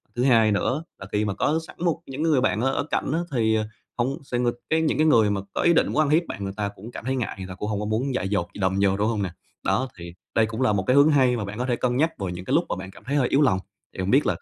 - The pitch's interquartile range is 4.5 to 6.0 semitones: Yes, average, 4.9 semitones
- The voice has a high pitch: No, low, 115 Hz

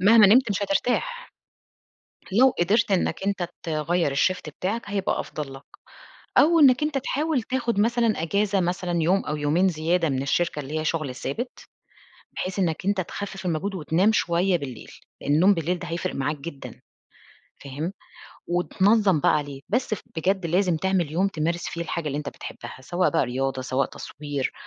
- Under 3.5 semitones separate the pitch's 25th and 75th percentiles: No, average, 4.7 semitones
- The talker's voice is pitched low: No, medium, 175 Hz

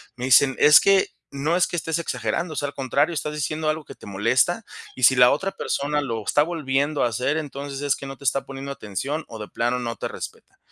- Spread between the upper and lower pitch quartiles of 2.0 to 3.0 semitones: No, average, 3.4 semitones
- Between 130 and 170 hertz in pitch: Yes, medium, 140 Hz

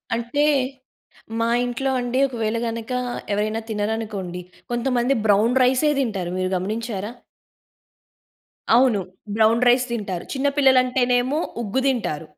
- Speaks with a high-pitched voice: Yes, high, 230 Hz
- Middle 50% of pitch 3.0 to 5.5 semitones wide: Yes, average, 3.3 semitones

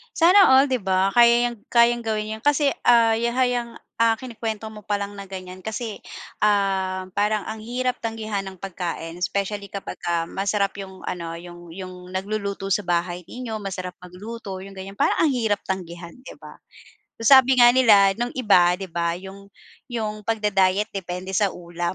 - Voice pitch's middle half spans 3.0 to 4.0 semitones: Yes, average, 3.6 semitones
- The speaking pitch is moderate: No, high, 200 Hz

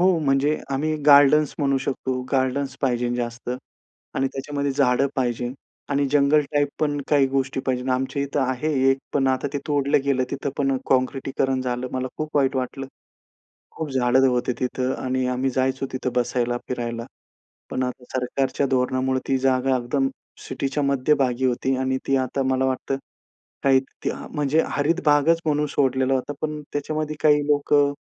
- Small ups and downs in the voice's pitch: Yes, narrow, 1.8 semitones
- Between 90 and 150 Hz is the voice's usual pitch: Yes, low, 135 Hz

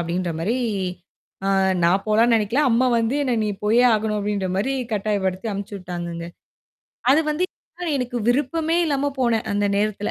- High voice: Yes, high, 215 Hz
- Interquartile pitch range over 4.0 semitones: Yes, average, 4.4 semitones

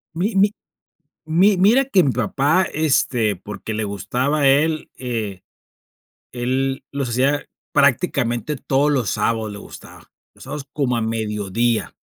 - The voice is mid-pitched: No, low, 130 Hz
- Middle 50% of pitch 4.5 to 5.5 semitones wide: Yes, average, 5.1 semitones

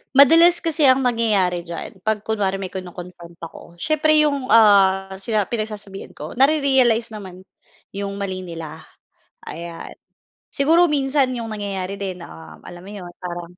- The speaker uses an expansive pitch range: Yes, wide, 6.0 semitones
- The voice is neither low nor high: No, high, 200 Hz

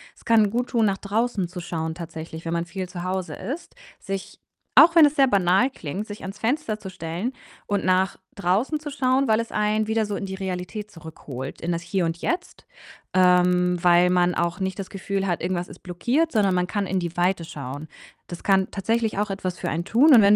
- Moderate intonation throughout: Yes, average, 3.7 semitones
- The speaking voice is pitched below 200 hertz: Yes, high, 190 Hz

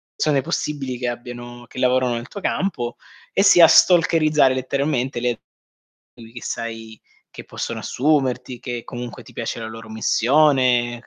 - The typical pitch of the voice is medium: No, low, 125 Hz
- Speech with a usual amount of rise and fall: Yes, average, 3.0 semitones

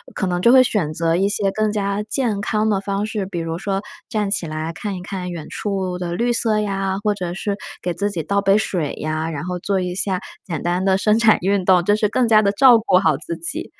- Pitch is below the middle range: No, high, 195 Hz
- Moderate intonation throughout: Yes, average, 3.0 semitones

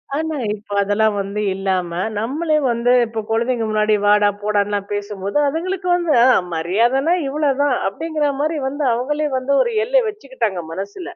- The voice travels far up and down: Yes, wide, 6.7 semitones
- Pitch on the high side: Yes, high, 235 Hz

